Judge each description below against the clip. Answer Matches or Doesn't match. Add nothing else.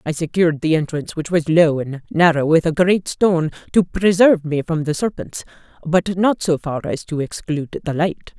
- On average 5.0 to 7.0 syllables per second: Matches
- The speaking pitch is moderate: Matches